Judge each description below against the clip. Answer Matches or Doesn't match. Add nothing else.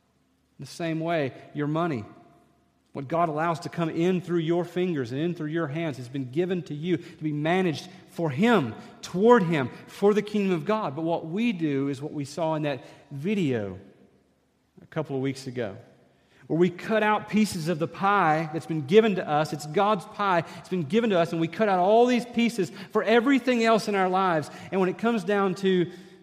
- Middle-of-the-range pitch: Matches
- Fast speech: Matches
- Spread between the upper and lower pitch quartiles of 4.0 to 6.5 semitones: Matches